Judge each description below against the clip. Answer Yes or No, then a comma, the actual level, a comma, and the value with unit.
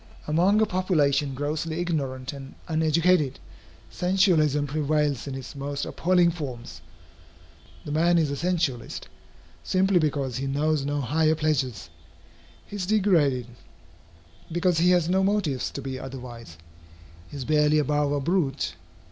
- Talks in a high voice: No, medium, 150 Hz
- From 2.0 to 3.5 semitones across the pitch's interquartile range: No, average, 4.2 semitones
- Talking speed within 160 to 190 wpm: No, slow, 135 wpm